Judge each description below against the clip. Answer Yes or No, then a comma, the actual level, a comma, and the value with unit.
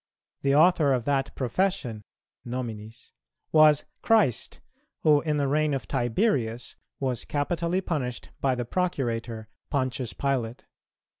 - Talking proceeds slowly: Yes, slow, 120 wpm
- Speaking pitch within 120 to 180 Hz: Yes, low, 135 Hz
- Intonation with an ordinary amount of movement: Yes, average, 4.2 semitones